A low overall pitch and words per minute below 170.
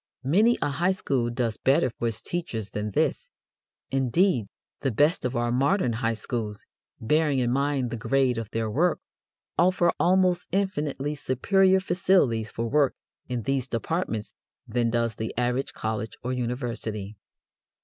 Yes: low, 125 Hz; average, 150 wpm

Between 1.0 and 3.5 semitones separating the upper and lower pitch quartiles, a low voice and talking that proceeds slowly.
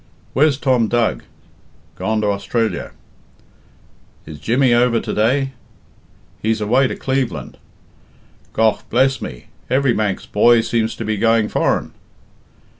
Yes: average, 3.0 semitones; low, 115 Hz; slow, 120 wpm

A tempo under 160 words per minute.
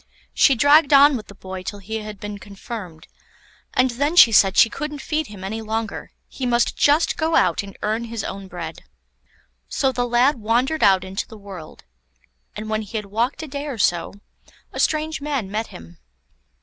No: average, 190 wpm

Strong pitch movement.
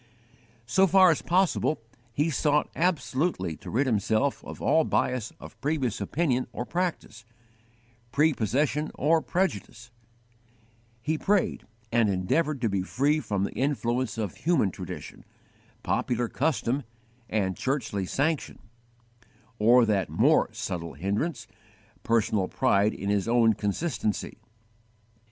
Yes: wide, 6.4 semitones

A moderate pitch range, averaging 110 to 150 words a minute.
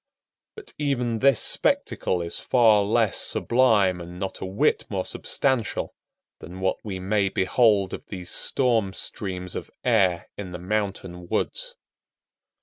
Yes: average, 4.3 semitones; average, 140 wpm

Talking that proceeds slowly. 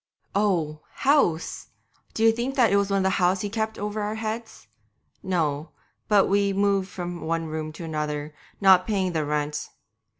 No: average, 155 wpm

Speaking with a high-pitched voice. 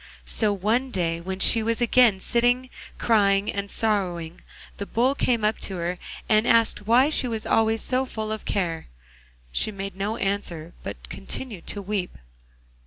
Yes: high, 210 Hz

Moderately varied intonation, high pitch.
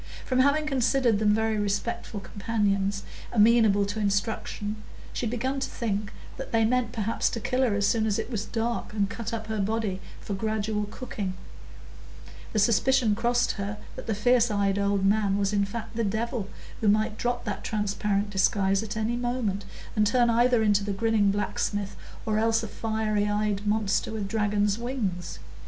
No: narrow, 2.2 semitones; high, 215 Hz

